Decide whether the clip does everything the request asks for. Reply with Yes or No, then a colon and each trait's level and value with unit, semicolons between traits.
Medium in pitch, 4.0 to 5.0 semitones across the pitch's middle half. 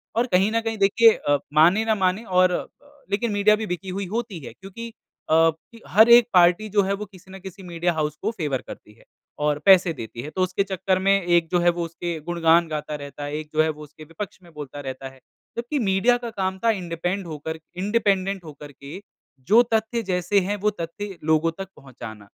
Yes: medium, 180 Hz; average, 4.5 semitones